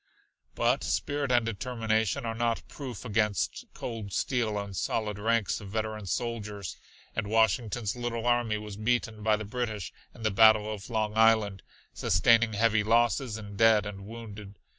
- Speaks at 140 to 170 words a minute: Yes, average, 155 wpm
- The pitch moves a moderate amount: No, narrow, 1.9 semitones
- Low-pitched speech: Yes, low, 110 Hz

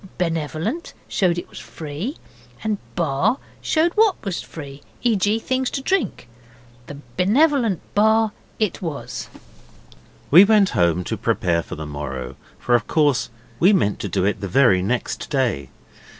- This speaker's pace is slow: No, average, 155 wpm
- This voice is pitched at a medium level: Yes, medium, 170 Hz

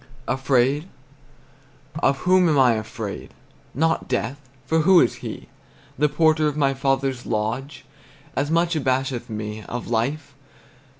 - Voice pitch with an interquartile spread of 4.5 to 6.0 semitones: No, average, 4.0 semitones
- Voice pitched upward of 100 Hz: Yes, low, 135 Hz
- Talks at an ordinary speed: No, slow, 130 wpm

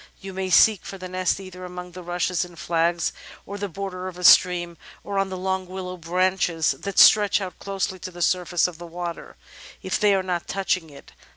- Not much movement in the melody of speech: Yes, narrow, 1.4 semitones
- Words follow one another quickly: Yes, fast, 210 wpm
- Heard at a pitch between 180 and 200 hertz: Yes, medium, 185 Hz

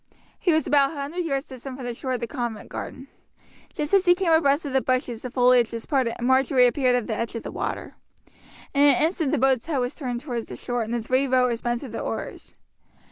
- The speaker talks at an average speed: No, fast, 240 wpm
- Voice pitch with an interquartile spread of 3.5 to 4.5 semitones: No, average, 2.8 semitones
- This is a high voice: Yes, very high, 260 Hz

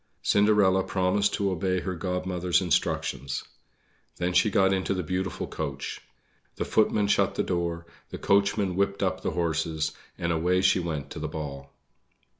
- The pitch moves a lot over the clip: No, average, 2.7 semitones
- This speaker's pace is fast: No, average, 155 wpm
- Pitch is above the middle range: No, very low, 90 Hz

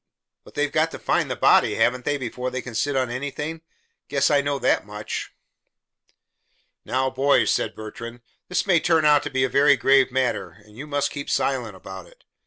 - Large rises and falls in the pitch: No, average, 2.7 semitones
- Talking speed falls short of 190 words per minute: No, average, 195 wpm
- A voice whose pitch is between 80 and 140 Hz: Yes, low, 135 Hz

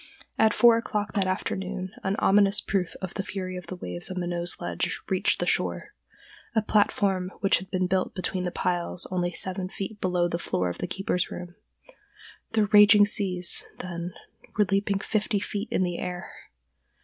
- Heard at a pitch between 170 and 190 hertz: Yes, medium, 185 Hz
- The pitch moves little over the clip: Yes, narrow, 2.2 semitones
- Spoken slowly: No, average, 175 wpm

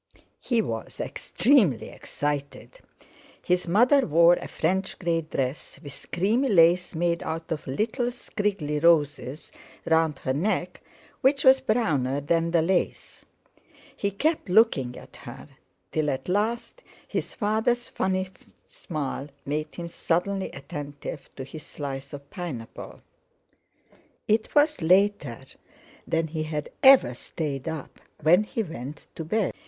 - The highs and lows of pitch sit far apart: Yes, wide, 6.0 semitones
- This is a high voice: No, medium, 170 Hz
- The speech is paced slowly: Yes, slow, 130 wpm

